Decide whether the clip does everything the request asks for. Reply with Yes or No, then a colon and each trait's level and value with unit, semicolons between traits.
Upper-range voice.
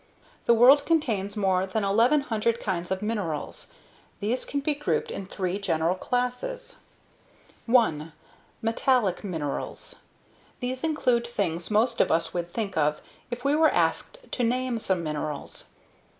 Yes: high, 215 Hz